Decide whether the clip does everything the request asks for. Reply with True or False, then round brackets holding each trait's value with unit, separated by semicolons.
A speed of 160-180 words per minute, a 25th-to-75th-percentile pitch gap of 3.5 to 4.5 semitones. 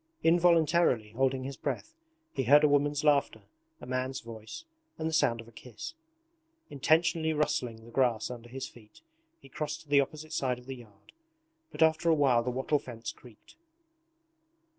True (170 wpm; 4.2 semitones)